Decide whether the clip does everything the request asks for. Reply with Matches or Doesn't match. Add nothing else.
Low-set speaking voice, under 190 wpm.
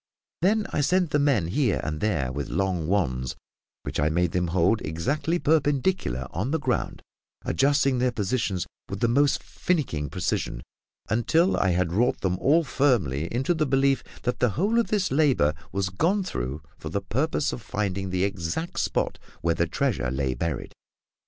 Matches